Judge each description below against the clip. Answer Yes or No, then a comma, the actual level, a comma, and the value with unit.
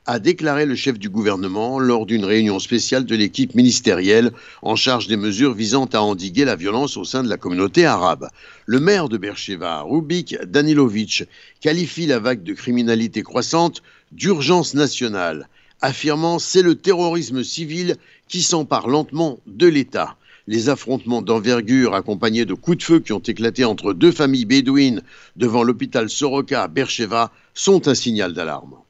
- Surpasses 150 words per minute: Yes, average, 160 wpm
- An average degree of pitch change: No, wide, 5.8 semitones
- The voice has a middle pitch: No, low, 130 Hz